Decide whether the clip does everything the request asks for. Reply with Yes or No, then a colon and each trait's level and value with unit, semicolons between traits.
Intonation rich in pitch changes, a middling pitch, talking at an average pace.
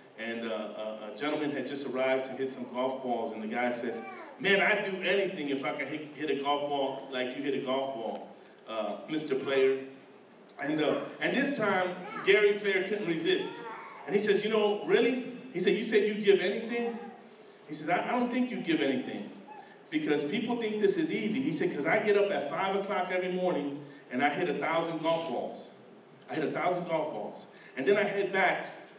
No: wide, 7.7 semitones; medium, 180 Hz; fast, 215 wpm